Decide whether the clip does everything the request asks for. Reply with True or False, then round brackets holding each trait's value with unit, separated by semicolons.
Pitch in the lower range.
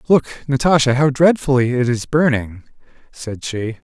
True (130 Hz)